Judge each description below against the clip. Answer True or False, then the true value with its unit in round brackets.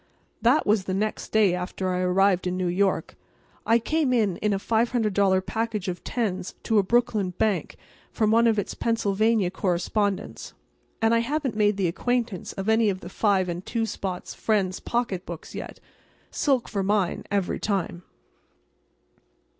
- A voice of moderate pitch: False (205 Hz)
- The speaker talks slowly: False (155 wpm)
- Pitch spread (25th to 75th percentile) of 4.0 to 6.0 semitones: False (3.4 semitones)